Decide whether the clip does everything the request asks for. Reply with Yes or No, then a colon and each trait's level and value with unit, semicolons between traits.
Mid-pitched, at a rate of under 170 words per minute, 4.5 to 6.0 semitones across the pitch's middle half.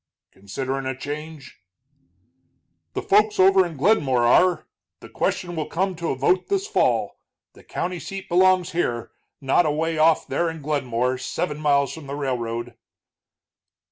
Yes: medium, 155 Hz; average, 145 wpm; average, 5.3 semitones